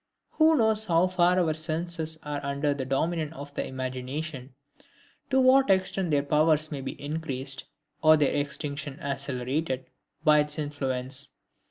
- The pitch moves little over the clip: No, average, 3.0 semitones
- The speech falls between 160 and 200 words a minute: No, average, 145 wpm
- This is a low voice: No, medium, 150 Hz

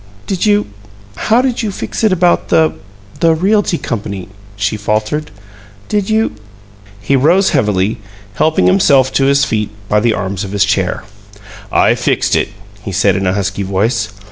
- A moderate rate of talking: Yes, average, 170 wpm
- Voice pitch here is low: Yes, low, 110 Hz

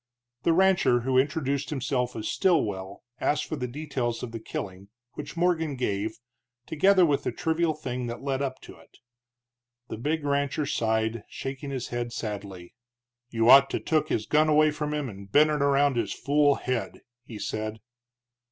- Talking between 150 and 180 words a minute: Yes, average, 170 wpm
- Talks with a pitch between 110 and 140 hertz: Yes, low, 135 Hz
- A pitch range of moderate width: Yes, average, 4.6 semitones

